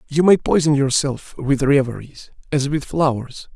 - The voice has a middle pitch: Yes, medium, 145 Hz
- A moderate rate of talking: Yes, average, 150 wpm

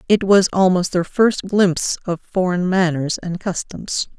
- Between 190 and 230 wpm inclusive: No, average, 160 wpm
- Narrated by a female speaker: Yes, female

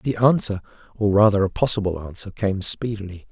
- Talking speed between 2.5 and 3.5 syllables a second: No, 5.4 syllables/s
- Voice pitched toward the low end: Yes, low, 105 Hz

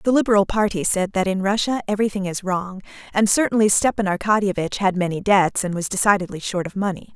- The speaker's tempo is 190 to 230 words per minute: Yes, average, 195 wpm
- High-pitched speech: Yes, high, 195 Hz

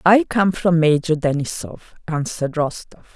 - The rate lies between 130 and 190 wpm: Yes, slow, 135 wpm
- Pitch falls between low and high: Yes, medium, 165 Hz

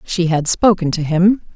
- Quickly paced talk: No, average, 195 wpm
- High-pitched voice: No, medium, 175 Hz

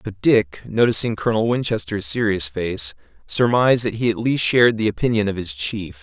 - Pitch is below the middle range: Yes, low, 105 Hz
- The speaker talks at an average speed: Yes, average, 180 wpm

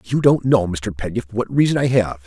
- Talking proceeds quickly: Yes, fast, 240 wpm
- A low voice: Yes, low, 110 Hz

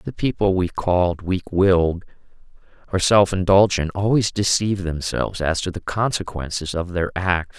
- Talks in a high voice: No, very low, 90 Hz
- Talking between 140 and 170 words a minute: Yes, average, 150 wpm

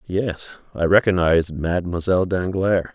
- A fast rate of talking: No, slow, 100 wpm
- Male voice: Yes, male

